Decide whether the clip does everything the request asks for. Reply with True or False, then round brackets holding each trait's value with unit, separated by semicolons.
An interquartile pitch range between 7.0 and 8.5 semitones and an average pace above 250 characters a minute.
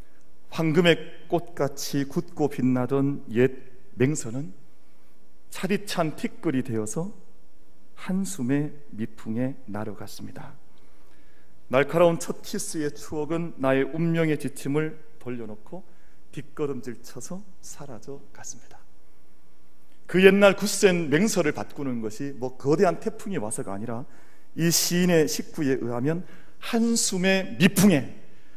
False (7.8 semitones; 240 characters per minute)